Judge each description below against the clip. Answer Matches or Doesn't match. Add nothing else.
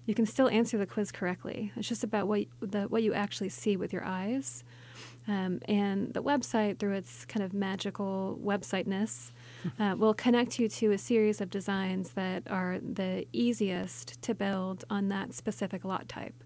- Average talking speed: Matches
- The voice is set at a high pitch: Matches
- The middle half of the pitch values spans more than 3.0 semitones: Doesn't match